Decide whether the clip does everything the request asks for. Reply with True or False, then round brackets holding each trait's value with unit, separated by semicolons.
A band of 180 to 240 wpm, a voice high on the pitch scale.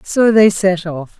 True (200 wpm; 195 Hz)